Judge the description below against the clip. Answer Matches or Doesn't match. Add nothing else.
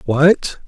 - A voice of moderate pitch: Matches